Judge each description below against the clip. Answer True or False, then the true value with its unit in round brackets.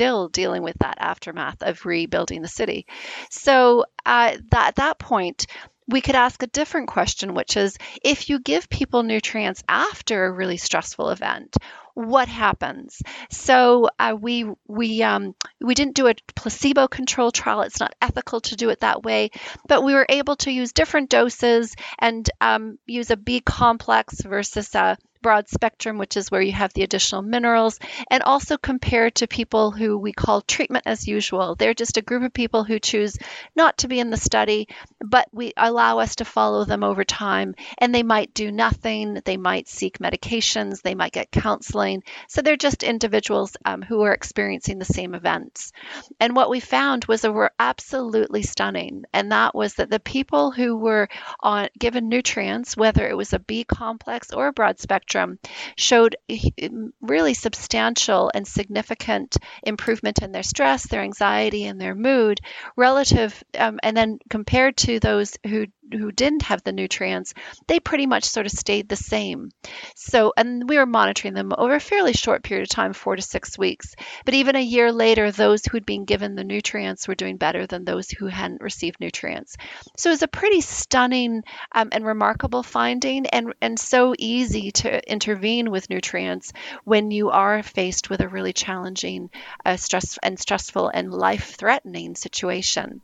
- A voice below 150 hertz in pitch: False (225 Hz)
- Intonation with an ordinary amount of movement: True (4.4 semitones)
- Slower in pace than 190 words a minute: True (175 wpm)